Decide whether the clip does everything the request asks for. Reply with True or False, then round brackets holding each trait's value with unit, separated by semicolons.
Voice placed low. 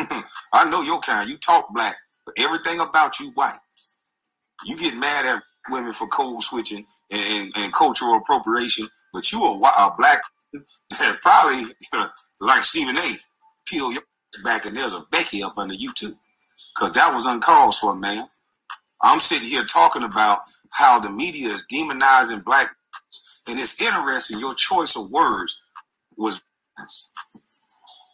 False (145 Hz)